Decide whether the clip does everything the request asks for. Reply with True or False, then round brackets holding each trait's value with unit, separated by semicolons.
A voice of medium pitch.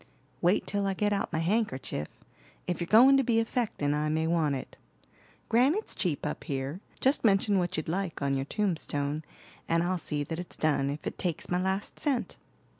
True (175 Hz)